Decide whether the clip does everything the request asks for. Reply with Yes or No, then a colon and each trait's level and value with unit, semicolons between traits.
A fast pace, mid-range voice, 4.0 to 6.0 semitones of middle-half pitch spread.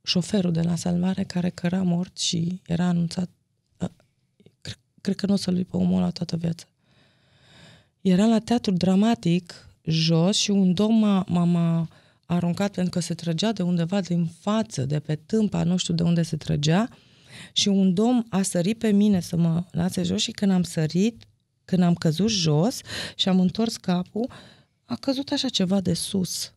No: fast, 180 wpm; medium, 180 Hz; average, 2.9 semitones